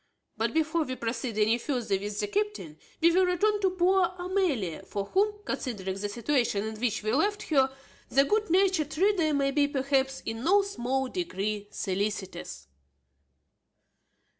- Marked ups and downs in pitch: Yes, wide, 8.9 semitones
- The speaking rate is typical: Yes, average, 155 wpm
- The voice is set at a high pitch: Yes, very high, 275 Hz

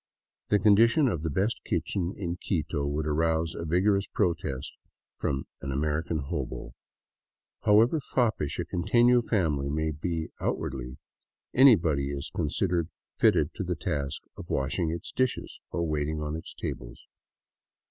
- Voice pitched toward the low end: Yes, very low, 80 Hz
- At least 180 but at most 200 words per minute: No, average, 145 wpm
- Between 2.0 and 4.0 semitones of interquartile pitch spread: No, average, 5.2 semitones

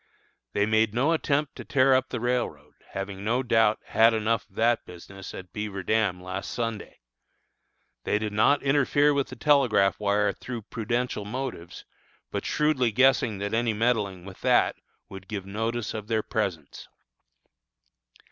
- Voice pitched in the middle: No, low, 110 Hz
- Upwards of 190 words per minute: No, average, 150 wpm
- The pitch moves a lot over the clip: No, average, 3.6 semitones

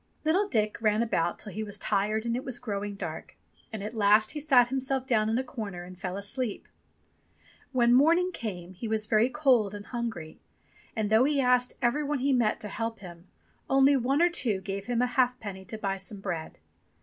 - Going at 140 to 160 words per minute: No, fast, 205 wpm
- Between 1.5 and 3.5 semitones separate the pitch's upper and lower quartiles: No, average, 4.0 semitones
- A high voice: Yes, high, 225 Hz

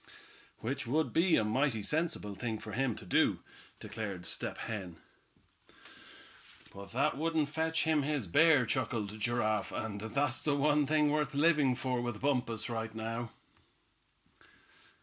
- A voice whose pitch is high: No, low, 125 Hz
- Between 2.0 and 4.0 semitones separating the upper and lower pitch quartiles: No, average, 5.2 semitones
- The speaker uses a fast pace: No, average, 140 wpm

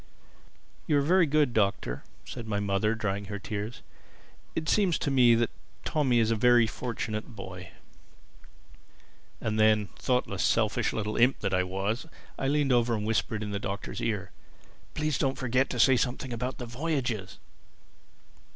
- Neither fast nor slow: Yes, average, 160 wpm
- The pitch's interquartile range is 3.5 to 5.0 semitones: Yes, average, 3.9 semitones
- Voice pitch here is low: Yes, low, 115 Hz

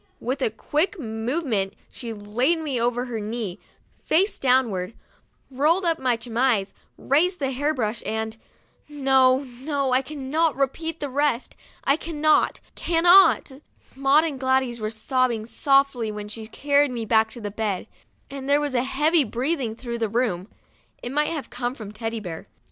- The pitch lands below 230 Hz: No, very high, 255 Hz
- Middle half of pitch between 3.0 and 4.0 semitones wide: No, average, 4.5 semitones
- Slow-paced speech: No, average, 160 wpm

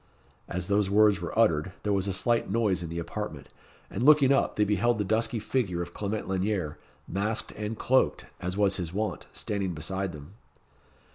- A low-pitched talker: Yes, low, 100 Hz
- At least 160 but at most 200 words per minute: Yes, average, 185 wpm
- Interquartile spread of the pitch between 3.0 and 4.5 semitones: Yes, average, 3.3 semitones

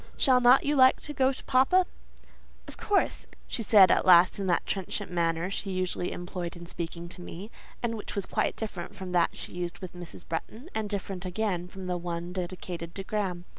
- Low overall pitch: No, medium, 185 Hz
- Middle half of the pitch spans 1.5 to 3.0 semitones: No, average, 3.8 semitones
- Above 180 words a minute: Yes, fast, 205 wpm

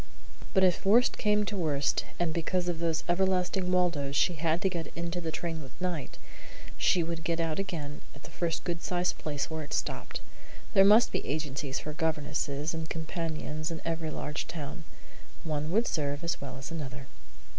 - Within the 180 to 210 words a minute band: Yes, average, 185 wpm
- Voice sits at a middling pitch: Yes, medium, 165 Hz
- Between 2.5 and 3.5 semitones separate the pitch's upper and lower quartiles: Yes, average, 2.9 semitones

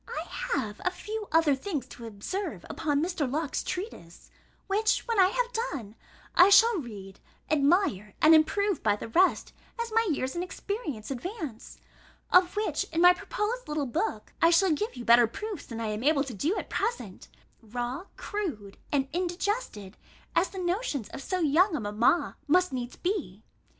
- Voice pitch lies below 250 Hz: No, very high, 325 Hz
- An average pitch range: No, wide, 8.5 semitones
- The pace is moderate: Yes, average, 170 wpm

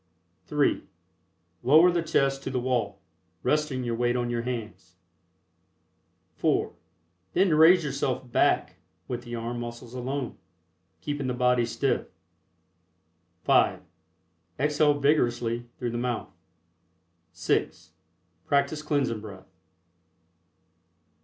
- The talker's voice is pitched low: Yes, low, 125 Hz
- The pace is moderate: No, slow, 105 wpm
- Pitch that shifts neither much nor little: Yes, average, 3.3 semitones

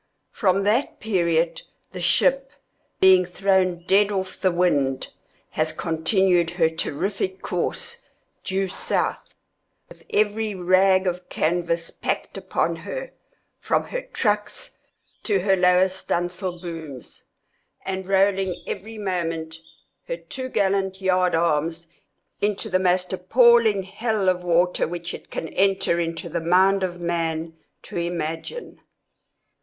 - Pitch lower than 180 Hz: No, medium, 185 Hz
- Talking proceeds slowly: Yes, slow, 130 wpm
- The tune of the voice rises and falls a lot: No, narrow, 2.4 semitones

